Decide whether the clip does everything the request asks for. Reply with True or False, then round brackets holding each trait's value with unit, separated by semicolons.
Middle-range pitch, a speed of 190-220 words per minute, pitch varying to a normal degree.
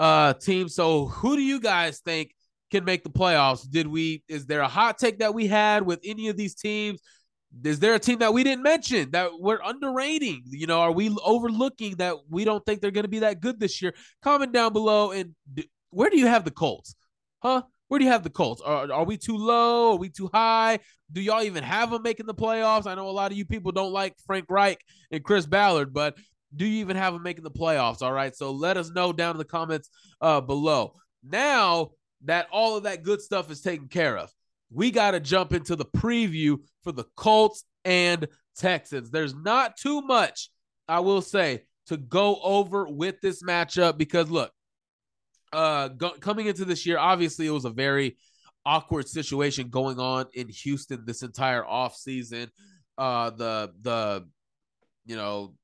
False (180 Hz; 205 wpm; 6.1 semitones)